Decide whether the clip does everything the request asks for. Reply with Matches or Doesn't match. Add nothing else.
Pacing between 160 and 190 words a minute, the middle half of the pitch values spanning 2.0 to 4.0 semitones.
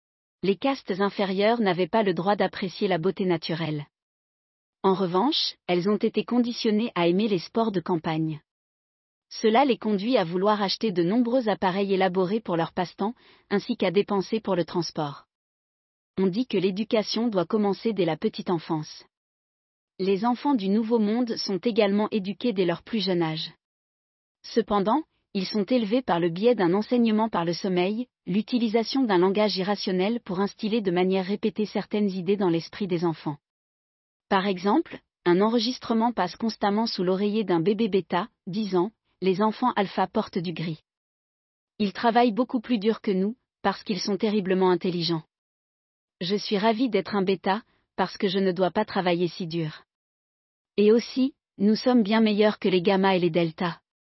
Matches